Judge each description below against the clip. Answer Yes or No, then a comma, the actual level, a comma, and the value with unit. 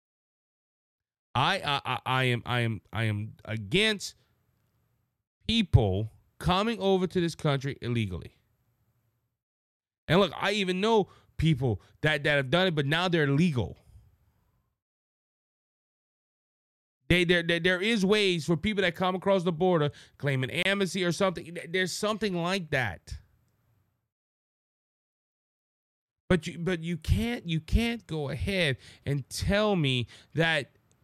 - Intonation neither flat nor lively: No, wide, 8.2 semitones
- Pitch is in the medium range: Yes, medium, 145 Hz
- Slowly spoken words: Yes, slow, 125 wpm